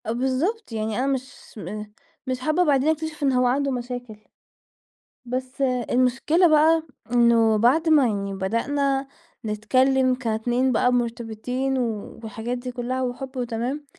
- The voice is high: Yes, very high, 255 Hz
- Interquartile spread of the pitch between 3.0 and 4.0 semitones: No, narrow, 2.5 semitones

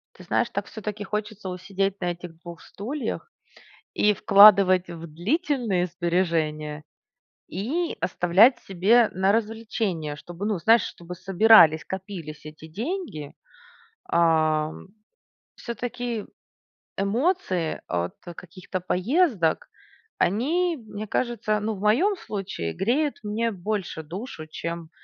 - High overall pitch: Yes, high, 195 Hz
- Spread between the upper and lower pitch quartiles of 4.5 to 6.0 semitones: Yes, average, 4.8 semitones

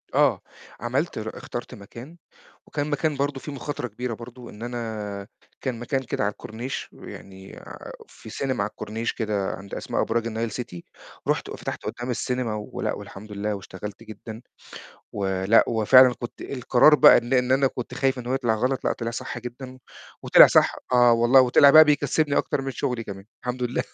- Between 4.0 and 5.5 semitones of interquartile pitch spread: No, average, 3.4 semitones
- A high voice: No, low, 120 Hz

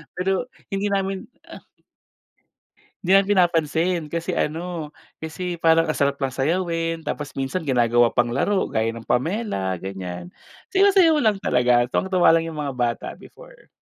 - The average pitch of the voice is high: No, medium, 165 Hz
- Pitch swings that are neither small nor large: No, wide, 6.8 semitones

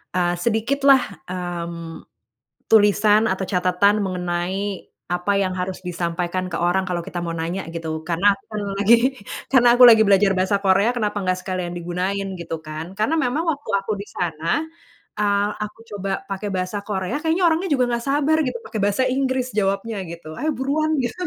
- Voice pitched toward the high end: Yes, high, 195 Hz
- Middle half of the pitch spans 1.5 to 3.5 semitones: No, average, 4.0 semitones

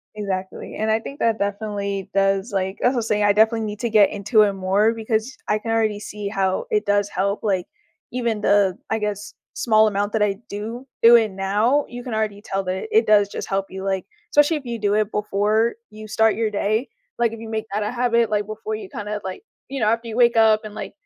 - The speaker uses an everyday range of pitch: No, narrow, 2.1 semitones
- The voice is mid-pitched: No, high, 215 Hz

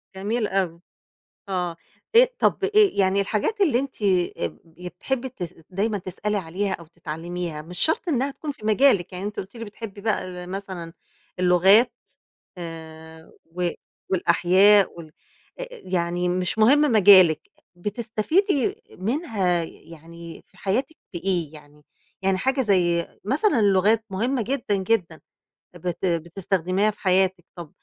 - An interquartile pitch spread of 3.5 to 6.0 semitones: Yes, average, 4.2 semitones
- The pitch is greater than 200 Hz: No, high, 190 Hz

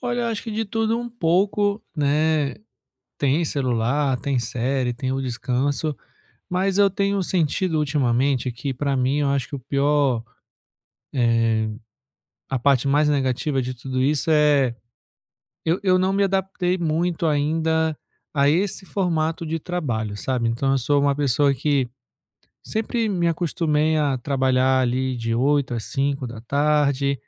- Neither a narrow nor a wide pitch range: Yes, average, 4.2 semitones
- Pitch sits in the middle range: Yes, medium, 145 Hz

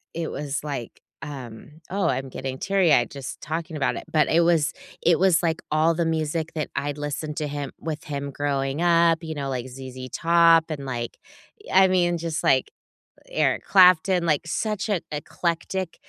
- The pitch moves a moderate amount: Yes, average, 3.3 semitones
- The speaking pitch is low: No, medium, 155 Hz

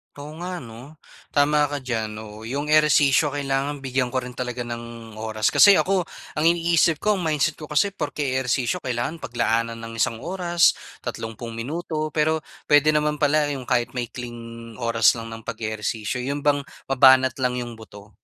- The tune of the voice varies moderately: Yes, average, 4.4 semitones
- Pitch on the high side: No, low, 130 Hz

